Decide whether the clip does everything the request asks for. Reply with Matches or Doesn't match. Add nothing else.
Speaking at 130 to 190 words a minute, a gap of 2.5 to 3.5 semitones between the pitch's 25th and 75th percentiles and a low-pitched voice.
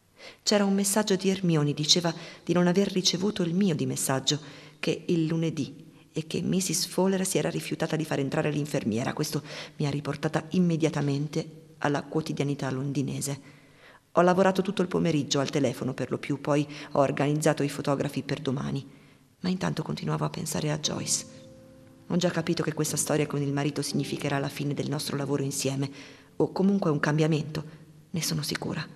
Doesn't match